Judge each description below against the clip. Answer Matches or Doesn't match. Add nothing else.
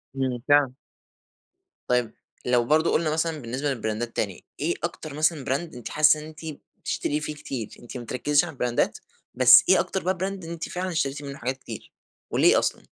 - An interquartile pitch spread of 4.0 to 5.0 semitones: Matches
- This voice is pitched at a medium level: Matches